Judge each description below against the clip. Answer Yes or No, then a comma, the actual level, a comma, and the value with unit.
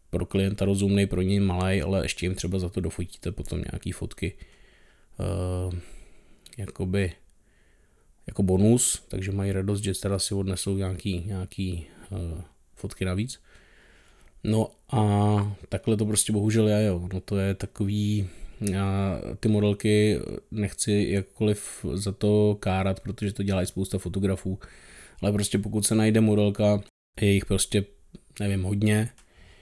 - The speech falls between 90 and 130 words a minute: No, average, 140 wpm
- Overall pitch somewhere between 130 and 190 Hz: No, low, 100 Hz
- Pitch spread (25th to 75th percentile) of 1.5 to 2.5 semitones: Yes, narrow, 2.0 semitones